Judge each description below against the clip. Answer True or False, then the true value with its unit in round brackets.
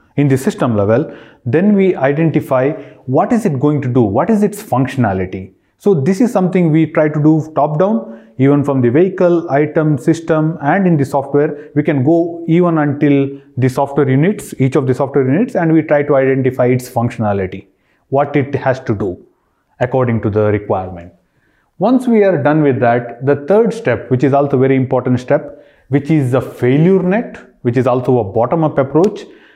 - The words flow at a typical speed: True (190 wpm)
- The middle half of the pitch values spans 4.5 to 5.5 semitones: False (4.0 semitones)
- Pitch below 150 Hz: True (140 Hz)